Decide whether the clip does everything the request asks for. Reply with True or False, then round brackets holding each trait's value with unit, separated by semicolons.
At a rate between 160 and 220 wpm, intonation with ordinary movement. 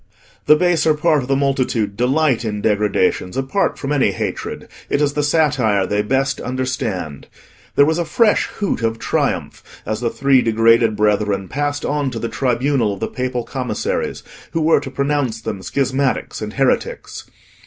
True (165 wpm; 4.6 semitones)